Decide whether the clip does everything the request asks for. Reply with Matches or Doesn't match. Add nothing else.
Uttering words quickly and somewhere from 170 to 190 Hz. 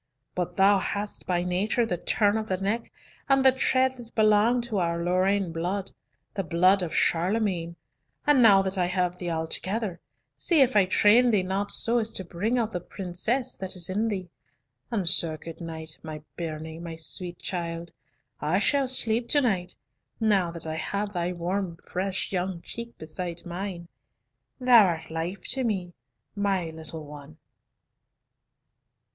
Doesn't match